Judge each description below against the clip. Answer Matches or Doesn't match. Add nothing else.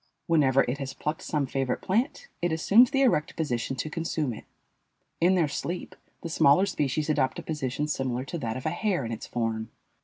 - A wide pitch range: Doesn't match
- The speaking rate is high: Doesn't match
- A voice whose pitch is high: Doesn't match